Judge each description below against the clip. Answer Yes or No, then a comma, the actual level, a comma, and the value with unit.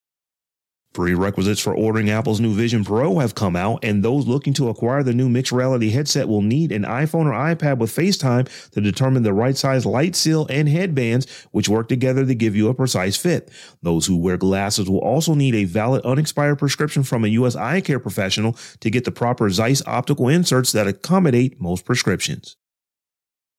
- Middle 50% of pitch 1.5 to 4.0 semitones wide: No, average, 4.8 semitones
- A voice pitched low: Yes, low, 125 Hz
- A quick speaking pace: No, average, 190 wpm